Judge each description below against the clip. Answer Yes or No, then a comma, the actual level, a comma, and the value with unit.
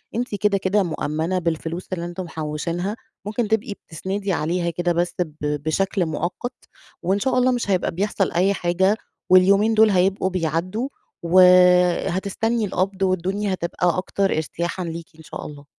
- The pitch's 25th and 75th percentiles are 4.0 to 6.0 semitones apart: No, average, 2.8 semitones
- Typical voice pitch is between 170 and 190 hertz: Yes, medium, 185 Hz